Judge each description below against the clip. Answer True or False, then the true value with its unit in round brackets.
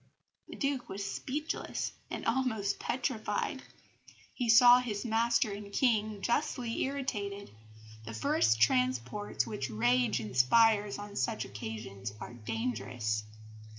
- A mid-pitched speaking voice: False (200 Hz)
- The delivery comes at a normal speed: False (115 wpm)